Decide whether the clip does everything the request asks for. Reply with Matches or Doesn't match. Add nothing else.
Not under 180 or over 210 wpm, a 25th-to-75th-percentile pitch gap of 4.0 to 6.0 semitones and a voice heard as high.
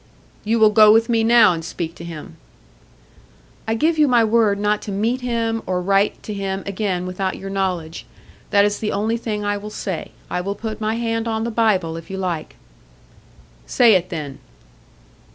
Doesn't match